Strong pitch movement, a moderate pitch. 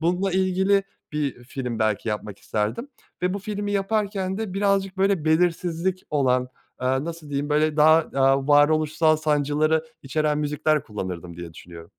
Yes: wide, 5.7 semitones; medium, 155 Hz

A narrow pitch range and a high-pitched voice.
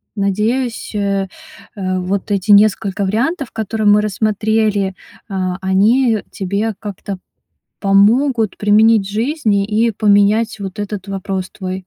Yes: narrow, 2.1 semitones; high, 205 Hz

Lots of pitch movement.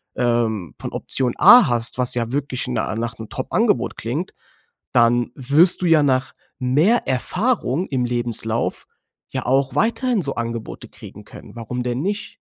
No: average, 3.8 semitones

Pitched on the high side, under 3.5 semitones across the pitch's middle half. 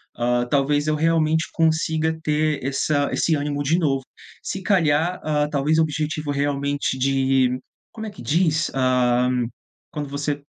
No: medium, 150 Hz; narrow, 2.4 semitones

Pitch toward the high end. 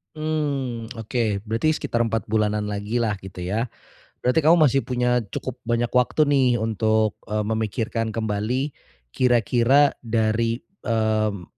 No: low, 115 Hz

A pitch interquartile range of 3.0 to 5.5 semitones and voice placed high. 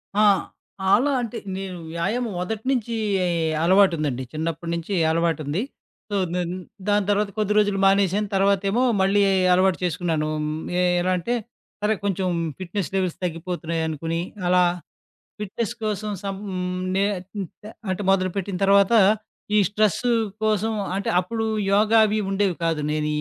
Yes: average, 3.3 semitones; high, 195 Hz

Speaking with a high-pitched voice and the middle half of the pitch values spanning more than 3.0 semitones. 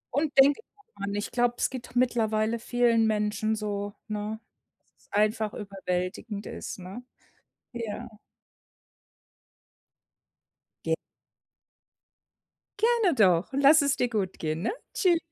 Yes: high, 220 Hz; average, 3.6 semitones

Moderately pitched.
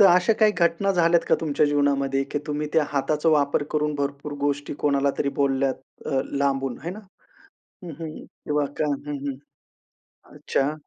Yes: medium, 145 Hz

